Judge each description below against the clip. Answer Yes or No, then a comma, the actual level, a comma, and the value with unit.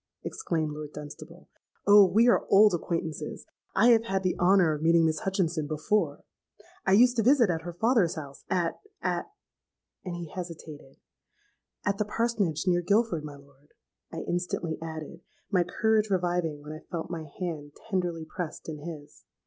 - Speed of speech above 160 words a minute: No, average, 155 wpm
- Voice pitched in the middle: Yes, medium, 175 Hz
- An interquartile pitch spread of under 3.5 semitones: No, average, 4.1 semitones